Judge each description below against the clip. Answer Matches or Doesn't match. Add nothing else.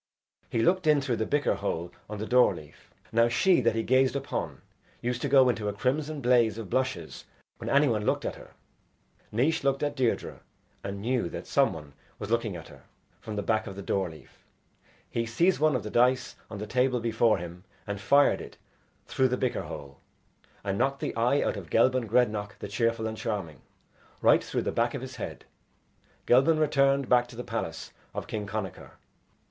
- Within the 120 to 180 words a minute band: Doesn't match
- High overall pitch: Doesn't match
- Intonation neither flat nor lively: Matches